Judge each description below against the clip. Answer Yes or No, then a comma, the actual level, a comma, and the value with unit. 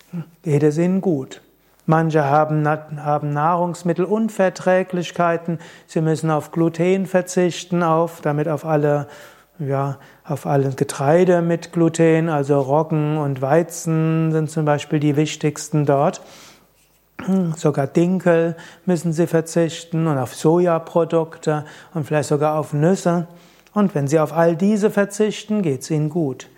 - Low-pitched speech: No, medium, 160 Hz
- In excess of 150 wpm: No, average, 130 wpm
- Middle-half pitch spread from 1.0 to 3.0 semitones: Yes, narrow, 2.4 semitones